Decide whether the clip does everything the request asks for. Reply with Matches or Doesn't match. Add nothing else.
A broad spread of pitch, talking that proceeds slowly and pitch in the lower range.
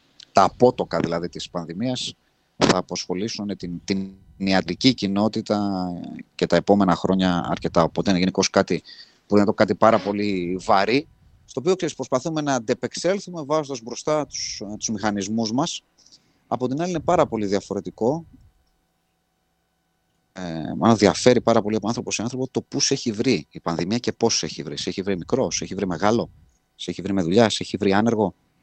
Doesn't match